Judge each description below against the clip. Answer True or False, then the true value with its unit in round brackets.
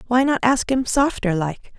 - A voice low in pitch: False (240 Hz)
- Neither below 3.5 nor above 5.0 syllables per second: True (4.6 syllables/s)